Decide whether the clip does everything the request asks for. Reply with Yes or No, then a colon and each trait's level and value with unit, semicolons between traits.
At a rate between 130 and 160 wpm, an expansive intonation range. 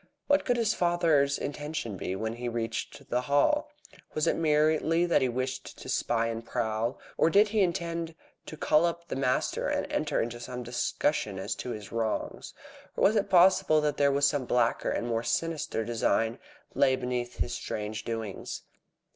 No: average, 170 wpm; wide, 6.1 semitones